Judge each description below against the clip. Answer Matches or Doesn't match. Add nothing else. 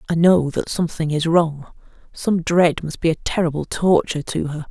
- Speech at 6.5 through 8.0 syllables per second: Doesn't match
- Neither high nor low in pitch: Matches